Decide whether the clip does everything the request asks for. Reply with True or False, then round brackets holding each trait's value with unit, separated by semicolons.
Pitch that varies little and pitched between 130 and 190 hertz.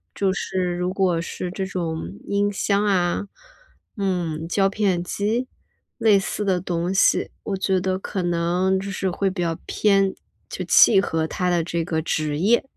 True (2.3 semitones; 185 Hz)